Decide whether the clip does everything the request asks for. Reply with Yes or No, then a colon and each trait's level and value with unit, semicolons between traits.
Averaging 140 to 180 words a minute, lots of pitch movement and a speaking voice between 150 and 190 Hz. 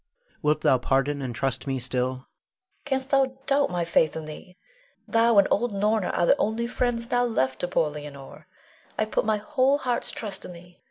No: average, 200 wpm; wide, 8.6 semitones; medium, 185 Hz